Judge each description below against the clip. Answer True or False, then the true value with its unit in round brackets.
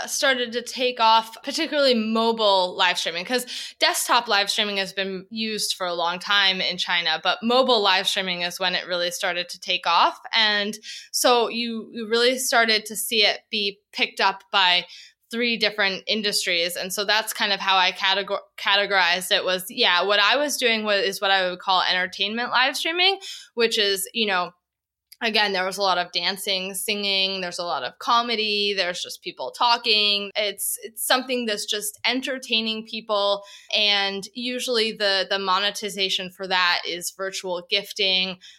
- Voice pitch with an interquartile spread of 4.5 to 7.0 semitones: False (3.7 semitones)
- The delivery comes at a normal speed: True (175 wpm)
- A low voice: False (205 Hz)